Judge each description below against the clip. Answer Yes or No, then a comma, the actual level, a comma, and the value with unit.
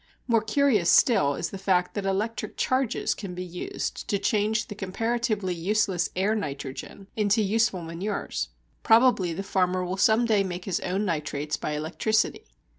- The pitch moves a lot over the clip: No, average, 3.4 semitones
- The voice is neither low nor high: No, high, 195 Hz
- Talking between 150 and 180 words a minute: Yes, average, 160 wpm